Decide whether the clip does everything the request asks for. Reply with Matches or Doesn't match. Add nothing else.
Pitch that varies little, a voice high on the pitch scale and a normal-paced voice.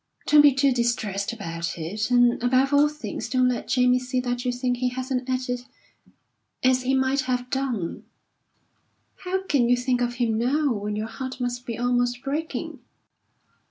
Matches